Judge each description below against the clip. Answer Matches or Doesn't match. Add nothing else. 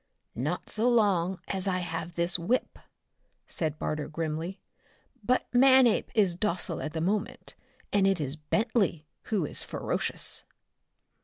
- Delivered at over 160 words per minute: Doesn't match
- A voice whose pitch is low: Doesn't match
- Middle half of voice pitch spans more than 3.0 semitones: Matches